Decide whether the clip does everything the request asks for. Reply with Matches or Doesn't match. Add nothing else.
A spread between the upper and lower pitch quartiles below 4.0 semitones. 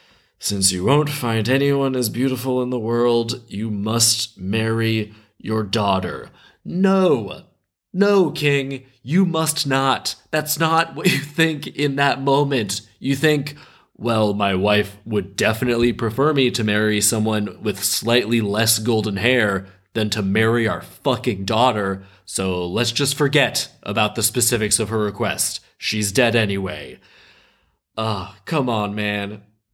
Doesn't match